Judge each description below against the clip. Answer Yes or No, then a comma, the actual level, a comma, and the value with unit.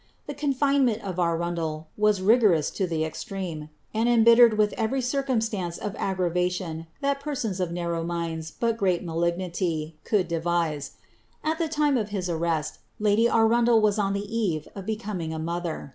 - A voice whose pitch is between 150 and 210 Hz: Yes, high, 190 Hz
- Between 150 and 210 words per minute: Yes, average, 160 wpm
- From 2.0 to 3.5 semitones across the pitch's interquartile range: No, average, 5.1 semitones